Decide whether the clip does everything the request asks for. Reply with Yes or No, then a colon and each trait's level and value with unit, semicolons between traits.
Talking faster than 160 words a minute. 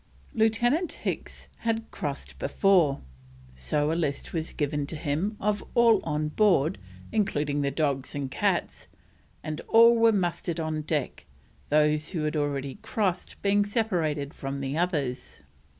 No: average, 140 wpm